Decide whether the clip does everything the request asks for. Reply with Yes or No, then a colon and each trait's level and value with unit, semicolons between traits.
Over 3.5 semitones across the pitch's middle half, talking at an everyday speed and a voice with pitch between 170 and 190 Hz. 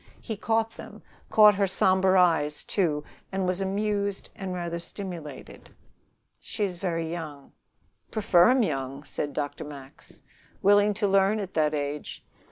Yes: average, 5.0 semitones; average, 145 wpm; medium, 185 Hz